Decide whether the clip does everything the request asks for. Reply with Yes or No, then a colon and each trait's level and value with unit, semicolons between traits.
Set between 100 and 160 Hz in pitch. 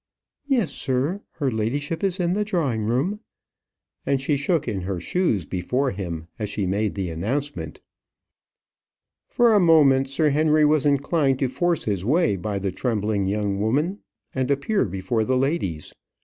Yes: low, 135 Hz